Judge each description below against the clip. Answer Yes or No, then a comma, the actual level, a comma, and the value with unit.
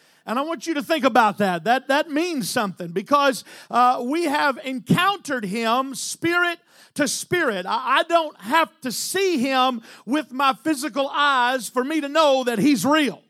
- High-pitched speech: Yes, very high, 270 Hz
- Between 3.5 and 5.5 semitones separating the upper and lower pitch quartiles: Yes, average, 3.9 semitones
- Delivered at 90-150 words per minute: No, average, 175 wpm